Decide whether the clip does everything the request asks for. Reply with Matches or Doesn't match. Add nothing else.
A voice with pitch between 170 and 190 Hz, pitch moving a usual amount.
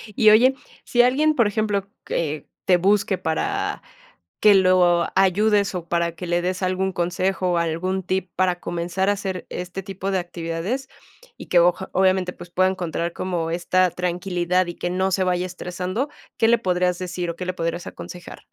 Doesn't match